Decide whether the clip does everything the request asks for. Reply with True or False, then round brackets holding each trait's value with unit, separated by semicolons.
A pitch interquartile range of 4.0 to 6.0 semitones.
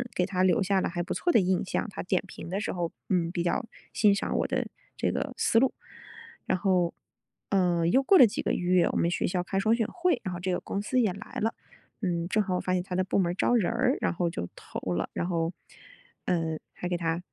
False (2.8 semitones)